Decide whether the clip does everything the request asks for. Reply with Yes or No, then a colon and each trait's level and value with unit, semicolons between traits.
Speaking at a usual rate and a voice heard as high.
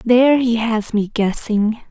Yes: average, 160 wpm; high, 225 Hz